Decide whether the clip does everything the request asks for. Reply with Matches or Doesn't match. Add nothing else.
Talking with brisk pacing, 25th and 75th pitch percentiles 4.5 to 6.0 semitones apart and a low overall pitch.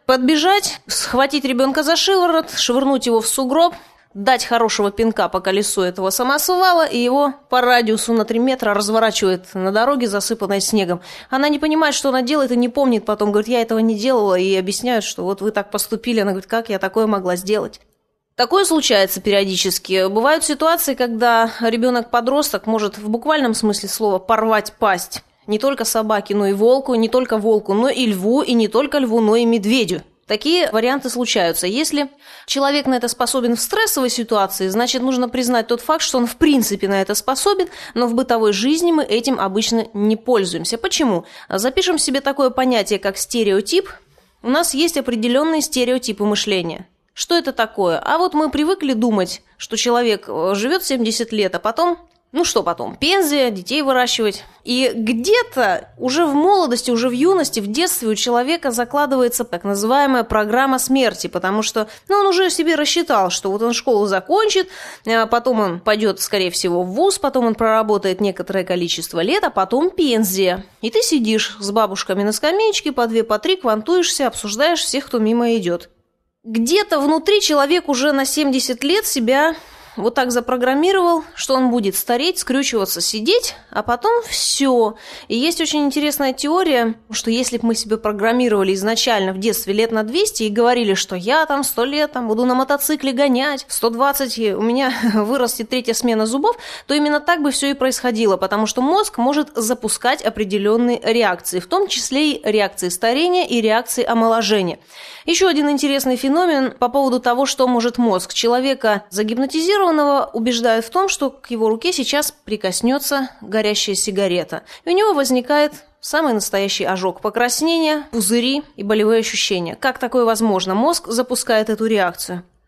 Doesn't match